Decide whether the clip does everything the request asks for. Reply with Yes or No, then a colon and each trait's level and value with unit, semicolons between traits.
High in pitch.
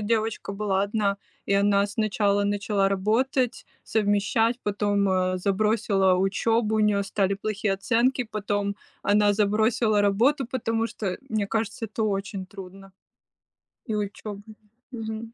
Yes: high, 205 Hz